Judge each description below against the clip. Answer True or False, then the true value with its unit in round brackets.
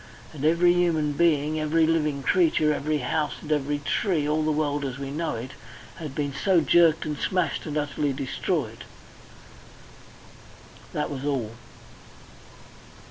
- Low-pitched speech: False (150 Hz)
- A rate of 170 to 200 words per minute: False (140 wpm)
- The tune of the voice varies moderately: False (2.1 semitones)